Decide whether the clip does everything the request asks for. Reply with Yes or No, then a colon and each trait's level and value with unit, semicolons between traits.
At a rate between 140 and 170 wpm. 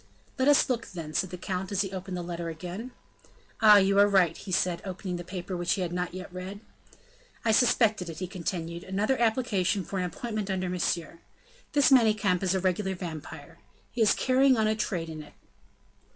No: average, 200 wpm